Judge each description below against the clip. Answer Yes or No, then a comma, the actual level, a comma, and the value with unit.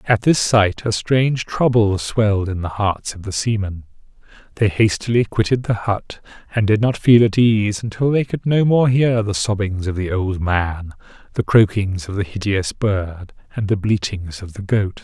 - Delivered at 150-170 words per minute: No, average, 190 wpm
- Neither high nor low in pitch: No, low, 105 Hz